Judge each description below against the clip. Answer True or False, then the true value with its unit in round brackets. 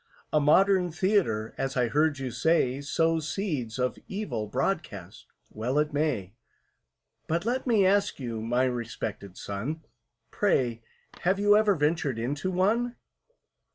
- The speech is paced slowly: True (130 wpm)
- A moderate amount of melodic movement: False (7.6 semitones)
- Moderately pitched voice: True (150 Hz)